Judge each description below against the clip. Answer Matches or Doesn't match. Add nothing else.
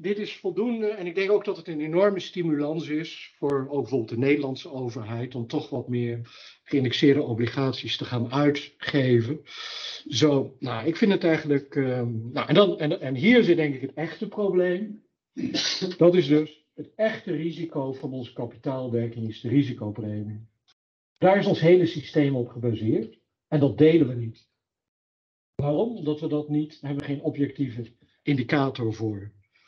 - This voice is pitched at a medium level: Matches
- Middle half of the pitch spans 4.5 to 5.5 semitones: Matches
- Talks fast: Doesn't match